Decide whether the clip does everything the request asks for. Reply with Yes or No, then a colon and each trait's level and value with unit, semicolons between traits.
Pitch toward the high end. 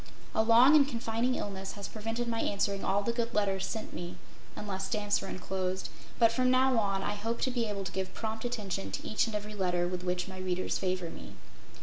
Yes: high, 205 Hz